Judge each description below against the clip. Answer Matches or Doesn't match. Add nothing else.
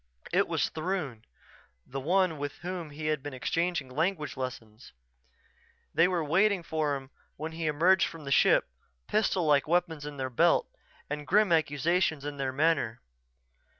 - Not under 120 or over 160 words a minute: Matches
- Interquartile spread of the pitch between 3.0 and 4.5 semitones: Matches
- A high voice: Doesn't match